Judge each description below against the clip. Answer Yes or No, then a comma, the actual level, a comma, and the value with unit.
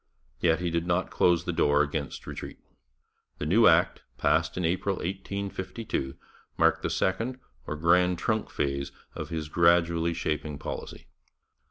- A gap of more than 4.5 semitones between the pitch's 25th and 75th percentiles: No, average, 3.2 semitones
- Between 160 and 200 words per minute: No, average, 145 wpm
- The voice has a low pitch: Yes, very low, 85 Hz